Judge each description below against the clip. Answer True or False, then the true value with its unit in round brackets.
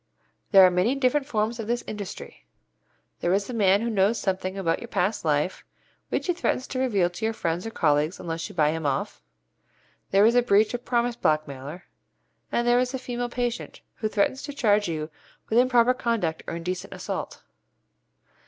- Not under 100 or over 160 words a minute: False (190 wpm)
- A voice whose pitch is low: False (210 Hz)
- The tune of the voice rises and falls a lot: True (5.7 semitones)